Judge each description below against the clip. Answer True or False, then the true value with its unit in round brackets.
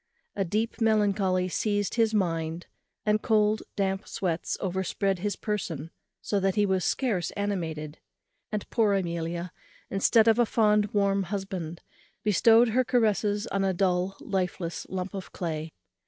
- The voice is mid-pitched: False (195 Hz)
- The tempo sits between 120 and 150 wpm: True (140 wpm)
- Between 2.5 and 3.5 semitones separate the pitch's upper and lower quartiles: True (2.9 semitones)